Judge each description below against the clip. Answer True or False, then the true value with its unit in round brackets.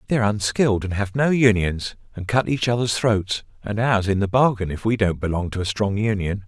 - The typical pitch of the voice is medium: False (105 Hz)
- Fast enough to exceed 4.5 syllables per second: True (5.4 syllables/s)